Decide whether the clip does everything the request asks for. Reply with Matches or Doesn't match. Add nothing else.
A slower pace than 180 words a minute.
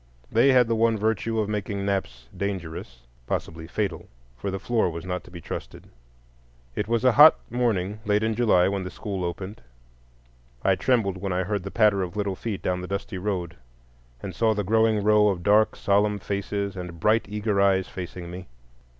Doesn't match